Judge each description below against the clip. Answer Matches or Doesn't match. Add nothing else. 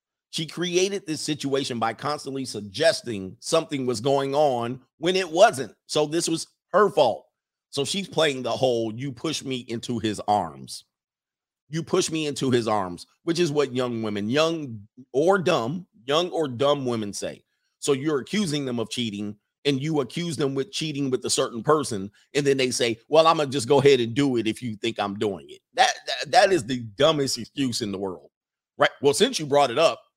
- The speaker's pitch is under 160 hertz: Matches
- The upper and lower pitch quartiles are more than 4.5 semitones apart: Matches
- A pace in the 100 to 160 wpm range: Doesn't match